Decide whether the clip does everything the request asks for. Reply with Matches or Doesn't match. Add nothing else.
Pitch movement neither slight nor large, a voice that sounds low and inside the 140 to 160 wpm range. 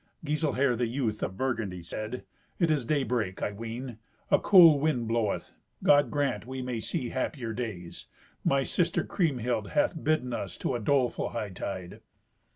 Matches